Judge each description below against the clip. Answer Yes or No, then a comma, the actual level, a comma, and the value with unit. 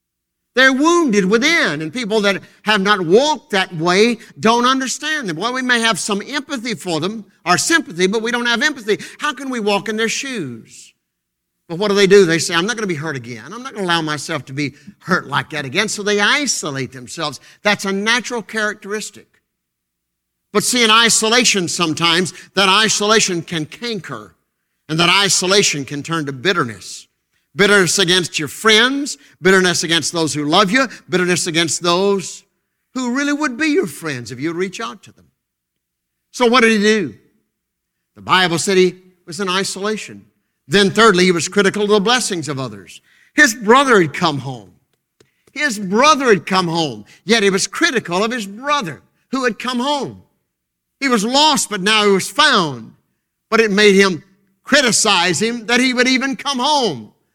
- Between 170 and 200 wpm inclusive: Yes, average, 185 wpm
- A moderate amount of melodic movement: No, wide, 5.8 semitones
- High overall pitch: Yes, high, 200 Hz